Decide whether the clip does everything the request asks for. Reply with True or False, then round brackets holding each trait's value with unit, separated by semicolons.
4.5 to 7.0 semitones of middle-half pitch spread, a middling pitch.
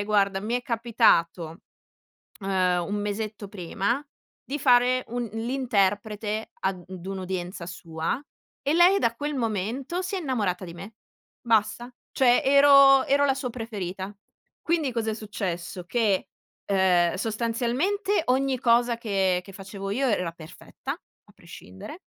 False (5.0 semitones; 220 Hz)